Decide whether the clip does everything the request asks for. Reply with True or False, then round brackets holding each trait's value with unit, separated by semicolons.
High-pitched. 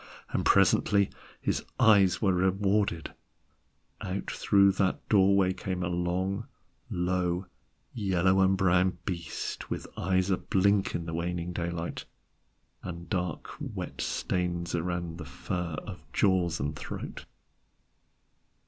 False (90 Hz)